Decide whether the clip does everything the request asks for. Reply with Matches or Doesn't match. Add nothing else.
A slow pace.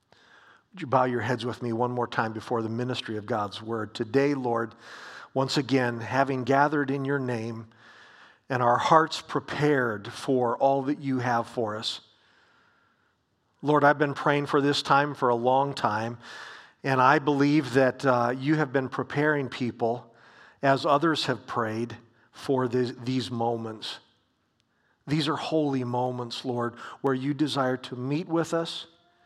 Doesn't match